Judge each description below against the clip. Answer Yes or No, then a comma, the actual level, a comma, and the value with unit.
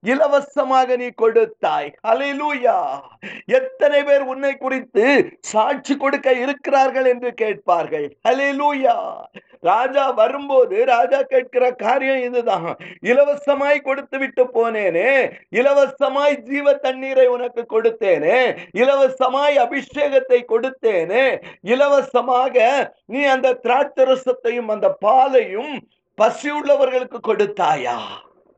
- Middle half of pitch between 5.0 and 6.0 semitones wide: No, narrow, 2.4 semitones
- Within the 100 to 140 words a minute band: No, average, 85 wpm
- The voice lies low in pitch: No, very high, 270 Hz